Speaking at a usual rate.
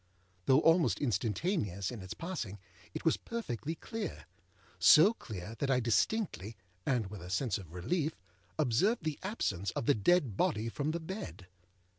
Yes: average, 155 wpm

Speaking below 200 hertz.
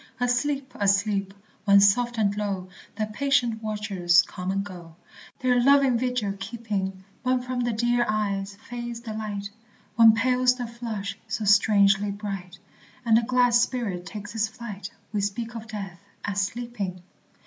No: high, 215 Hz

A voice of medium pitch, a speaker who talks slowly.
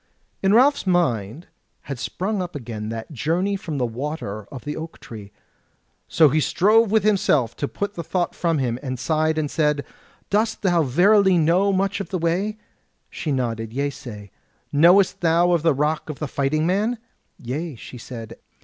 No: medium, 155 Hz; average, 175 wpm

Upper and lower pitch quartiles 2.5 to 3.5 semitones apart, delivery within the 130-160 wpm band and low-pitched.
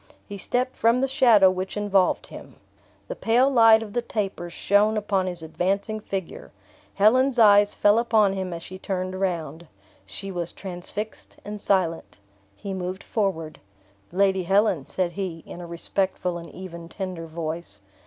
No: average, 3.2 semitones; average, 155 wpm; high, 195 Hz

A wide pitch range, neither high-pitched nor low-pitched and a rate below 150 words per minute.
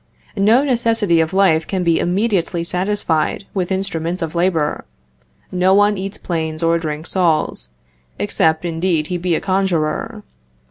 No: average, 3.2 semitones; medium, 180 Hz; average, 140 wpm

